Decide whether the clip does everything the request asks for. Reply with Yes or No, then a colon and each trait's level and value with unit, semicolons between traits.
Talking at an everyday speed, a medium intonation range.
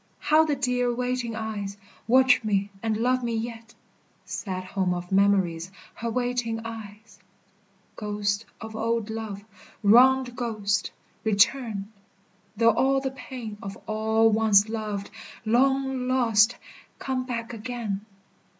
No: slow, 125 wpm; average, 3.1 semitones